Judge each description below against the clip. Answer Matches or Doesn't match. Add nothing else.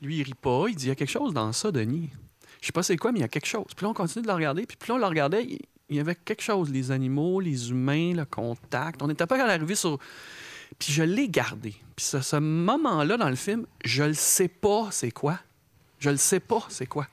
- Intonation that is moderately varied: Doesn't match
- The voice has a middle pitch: Matches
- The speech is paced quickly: Matches